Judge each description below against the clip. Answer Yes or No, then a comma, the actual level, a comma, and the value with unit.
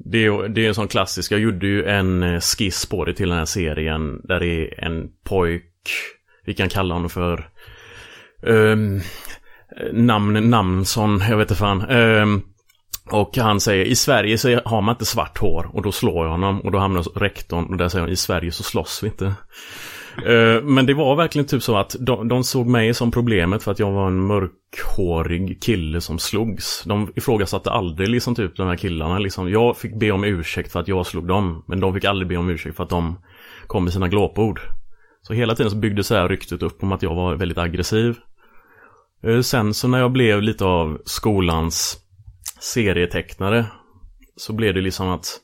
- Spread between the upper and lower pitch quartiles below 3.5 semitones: No, average, 3.9 semitones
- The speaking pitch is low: Yes, low, 100 Hz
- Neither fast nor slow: No, fast, 200 wpm